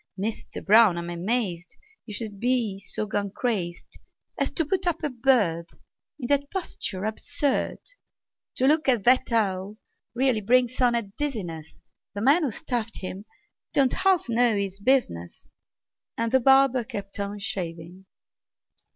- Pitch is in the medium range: No, high, 225 Hz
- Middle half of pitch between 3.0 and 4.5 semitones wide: No, average, 5.0 semitones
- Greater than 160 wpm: No, average, 145 wpm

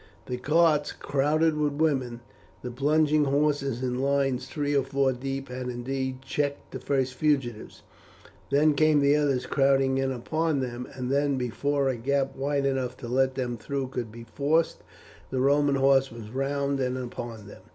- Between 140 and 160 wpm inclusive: No, average, 170 wpm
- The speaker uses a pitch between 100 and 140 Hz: Yes, low, 135 Hz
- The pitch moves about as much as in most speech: No, narrow, 2.1 semitones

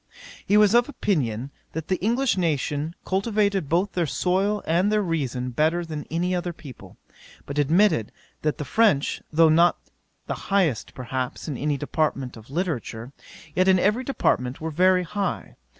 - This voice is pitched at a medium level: Yes, medium, 165 Hz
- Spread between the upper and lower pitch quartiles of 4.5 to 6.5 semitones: Yes, average, 5.2 semitones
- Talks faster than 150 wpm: Yes, average, 160 wpm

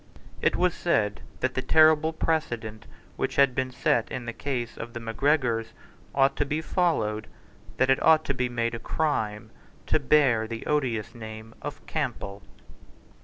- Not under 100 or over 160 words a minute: No, average, 170 wpm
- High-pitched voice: No, low, 125 Hz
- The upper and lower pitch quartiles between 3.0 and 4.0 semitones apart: No, average, 4.6 semitones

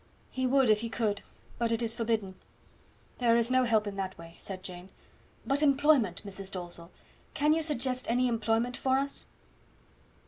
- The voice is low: No, high, 230 Hz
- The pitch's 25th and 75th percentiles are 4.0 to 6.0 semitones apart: Yes, average, 4.4 semitones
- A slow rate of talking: No, average, 170 wpm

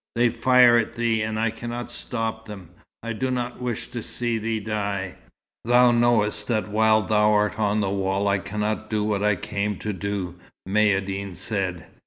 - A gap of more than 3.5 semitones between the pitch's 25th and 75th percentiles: No, narrow, 2.4 semitones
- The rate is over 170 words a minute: Yes, average, 180 wpm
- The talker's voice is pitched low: Yes, low, 105 Hz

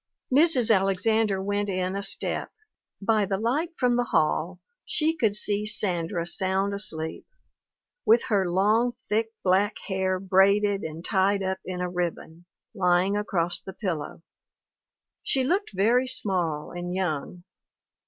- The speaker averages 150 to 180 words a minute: No, slow, 135 wpm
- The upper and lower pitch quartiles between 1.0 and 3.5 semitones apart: Yes, average, 3.1 semitones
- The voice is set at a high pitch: Yes, high, 195 Hz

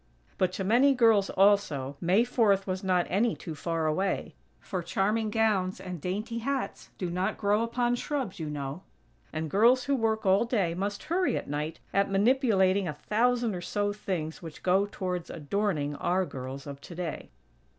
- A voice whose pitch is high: Yes, high, 195 Hz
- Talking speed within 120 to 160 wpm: No, average, 170 wpm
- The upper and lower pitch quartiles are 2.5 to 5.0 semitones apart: Yes, average, 4.5 semitones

